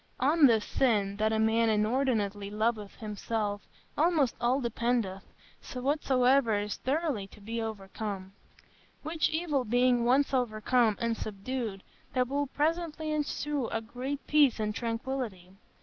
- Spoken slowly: Yes, slow, 125 wpm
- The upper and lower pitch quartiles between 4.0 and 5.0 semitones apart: Yes, average, 4.3 semitones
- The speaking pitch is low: No, high, 235 Hz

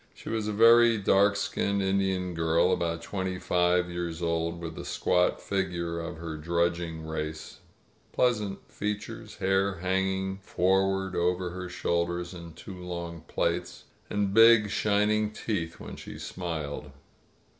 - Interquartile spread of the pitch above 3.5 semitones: No, narrow, 2.6 semitones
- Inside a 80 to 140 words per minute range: Yes, slow, 135 wpm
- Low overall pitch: Yes, very low, 90 Hz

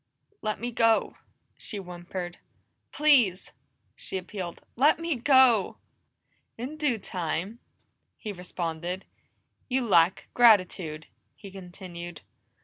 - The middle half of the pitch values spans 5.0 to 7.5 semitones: Yes, average, 5.3 semitones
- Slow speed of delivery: Yes, slow, 100 wpm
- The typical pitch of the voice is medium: No, high, 195 Hz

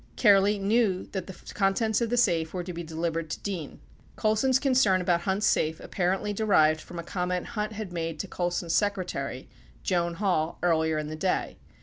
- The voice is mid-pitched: Yes, medium, 180 Hz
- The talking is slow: No, average, 190 wpm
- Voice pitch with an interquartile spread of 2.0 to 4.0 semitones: Yes, average, 3.7 semitones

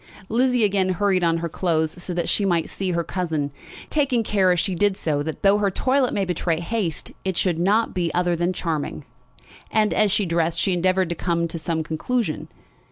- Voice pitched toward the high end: No, medium, 180 Hz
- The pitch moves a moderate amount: Yes, average, 3.4 semitones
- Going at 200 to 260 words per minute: Yes, fast, 205 wpm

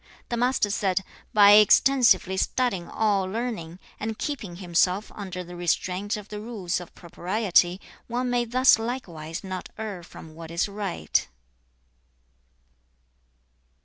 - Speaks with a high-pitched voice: Yes, high, 200 Hz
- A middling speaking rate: No, slow, 125 wpm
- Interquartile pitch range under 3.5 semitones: No, average, 4.1 semitones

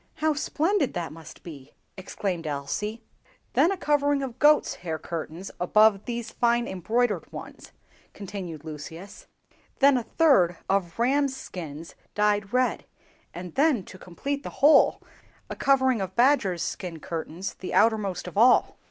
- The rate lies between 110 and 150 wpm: Yes, average, 145 wpm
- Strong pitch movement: Yes, wide, 7.2 semitones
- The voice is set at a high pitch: Yes, high, 205 Hz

